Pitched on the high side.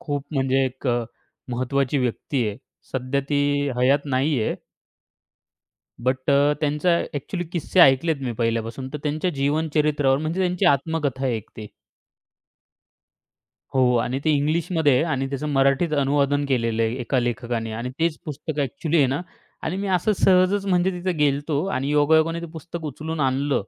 No: medium, 145 Hz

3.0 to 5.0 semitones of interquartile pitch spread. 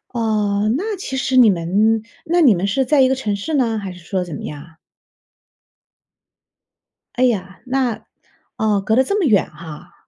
No: wide, 5.4 semitones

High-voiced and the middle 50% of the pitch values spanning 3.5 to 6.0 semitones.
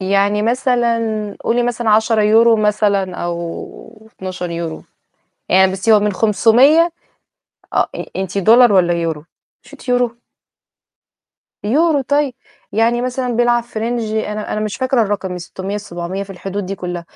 Yes: high, 215 Hz; average, 3.9 semitones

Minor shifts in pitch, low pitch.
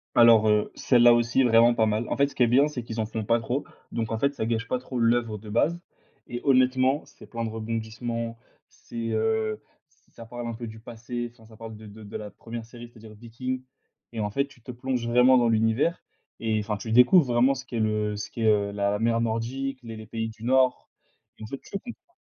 Yes: narrow, 2.0 semitones; low, 115 Hz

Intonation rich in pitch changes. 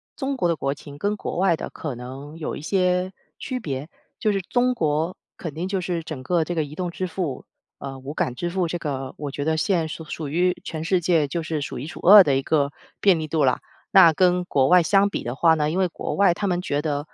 No: average, 3.8 semitones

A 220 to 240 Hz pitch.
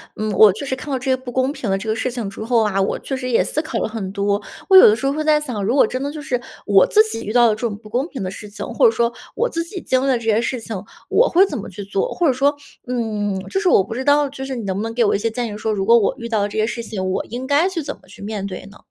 Yes: high, 235 Hz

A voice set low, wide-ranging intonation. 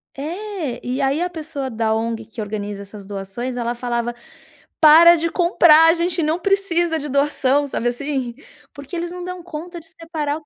No: very high, 295 Hz; wide, 6.0 semitones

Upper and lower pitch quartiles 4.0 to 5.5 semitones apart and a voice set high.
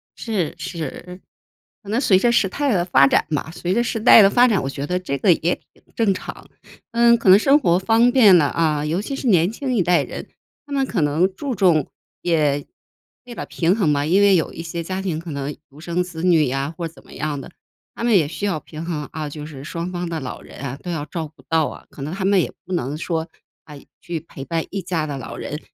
No: average, 4.6 semitones; medium, 175 Hz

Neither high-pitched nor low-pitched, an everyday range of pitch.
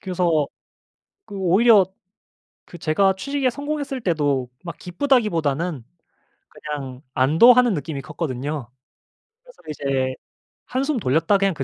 No: medium, 170 Hz; wide, 8.2 semitones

